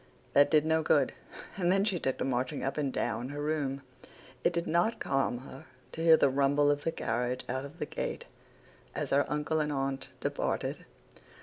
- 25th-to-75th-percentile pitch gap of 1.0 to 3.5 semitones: Yes, average, 2.8 semitones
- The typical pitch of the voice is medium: Yes, medium, 145 Hz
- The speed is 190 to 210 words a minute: Yes, average, 195 wpm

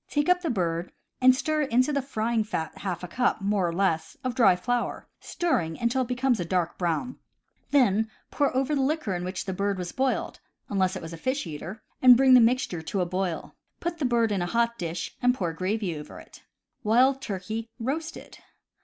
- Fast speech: Yes, fast, 210 wpm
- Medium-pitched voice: No, high, 220 Hz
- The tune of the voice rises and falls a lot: Yes, wide, 6.2 semitones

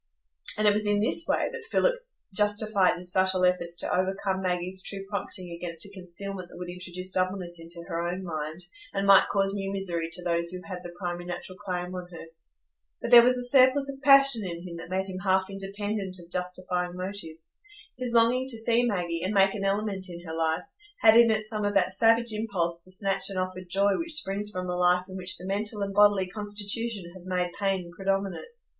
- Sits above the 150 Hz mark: Yes, high, 190 Hz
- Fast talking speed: Yes, fast, 210 wpm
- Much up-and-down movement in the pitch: No, narrow, 2.5 semitones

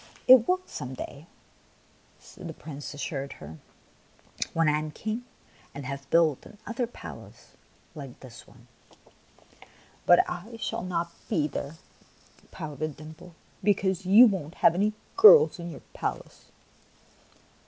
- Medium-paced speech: No, slow, 130 wpm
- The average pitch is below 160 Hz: No, medium, 165 Hz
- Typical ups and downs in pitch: No, wide, 6.1 semitones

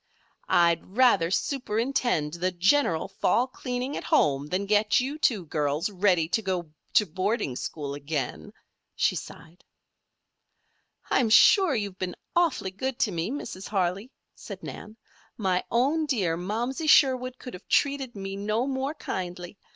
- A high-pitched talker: Yes, high, 205 Hz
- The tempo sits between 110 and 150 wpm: Yes, average, 145 wpm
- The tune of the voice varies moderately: No, wide, 6.4 semitones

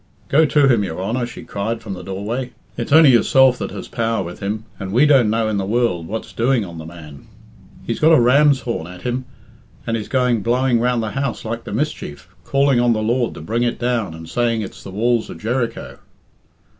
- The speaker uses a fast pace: Yes, fast, 220 wpm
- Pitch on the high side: No, low, 115 Hz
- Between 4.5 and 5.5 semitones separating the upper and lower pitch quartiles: No, average, 3.8 semitones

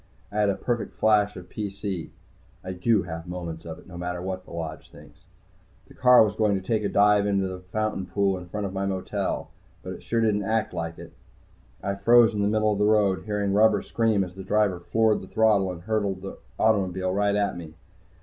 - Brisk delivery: Yes, fast, 220 wpm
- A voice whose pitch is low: Yes, low, 100 Hz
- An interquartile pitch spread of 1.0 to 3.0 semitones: Yes, narrow, 2.6 semitones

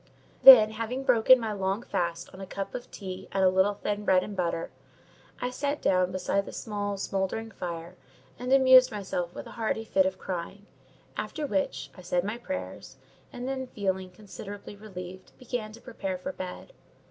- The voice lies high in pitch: Yes, high, 200 Hz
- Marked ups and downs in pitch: No, average, 3.6 semitones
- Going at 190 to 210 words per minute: No, average, 180 wpm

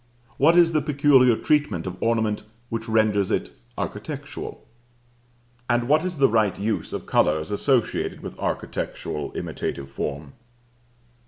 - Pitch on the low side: Yes, low, 115 Hz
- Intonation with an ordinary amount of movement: No, wide, 6.1 semitones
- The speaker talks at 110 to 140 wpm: Yes, slow, 135 wpm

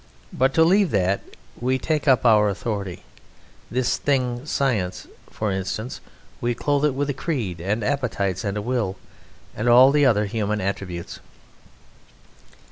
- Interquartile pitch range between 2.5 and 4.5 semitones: No, average, 5.0 semitones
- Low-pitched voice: Yes, low, 120 Hz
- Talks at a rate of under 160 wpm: Yes, average, 140 wpm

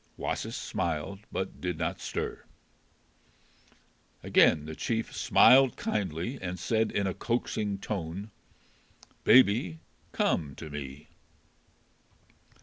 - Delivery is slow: Yes, slow, 100 wpm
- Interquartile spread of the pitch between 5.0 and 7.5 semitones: Yes, wide, 5.6 semitones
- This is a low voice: Yes, very low, 95 Hz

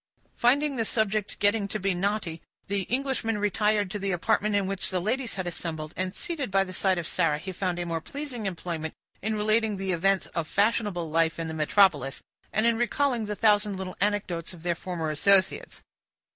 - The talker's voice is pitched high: Yes, high, 195 Hz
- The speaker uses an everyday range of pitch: Yes, average, 3.6 semitones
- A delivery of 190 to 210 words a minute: Yes, average, 195 wpm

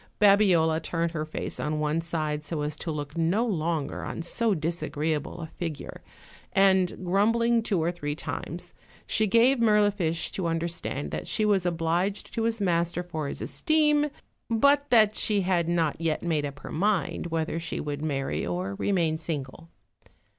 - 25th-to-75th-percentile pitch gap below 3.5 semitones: No, average, 4.5 semitones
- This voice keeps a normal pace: Yes, average, 165 wpm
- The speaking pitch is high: No, medium, 170 Hz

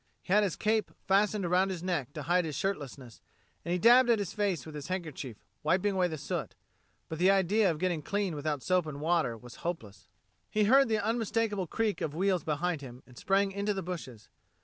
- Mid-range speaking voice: Yes, medium, 180 Hz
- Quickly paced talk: Yes, fast, 215 wpm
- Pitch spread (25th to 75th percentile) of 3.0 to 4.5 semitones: No, average, 4.9 semitones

